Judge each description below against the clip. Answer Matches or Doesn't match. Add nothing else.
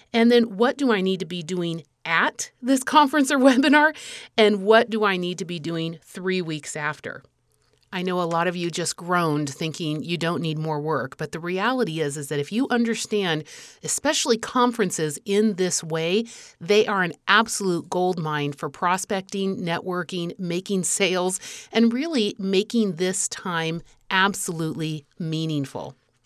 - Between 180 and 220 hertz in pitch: Matches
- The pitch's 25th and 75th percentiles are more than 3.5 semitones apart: Matches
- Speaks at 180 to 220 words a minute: Doesn't match